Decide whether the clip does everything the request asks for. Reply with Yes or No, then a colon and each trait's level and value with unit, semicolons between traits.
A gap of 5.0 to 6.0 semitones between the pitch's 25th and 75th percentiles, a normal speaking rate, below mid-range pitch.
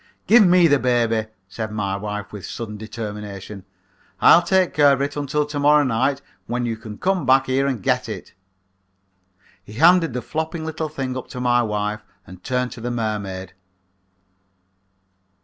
Yes: wide, 5.4 semitones; average, 165 wpm; low, 125 Hz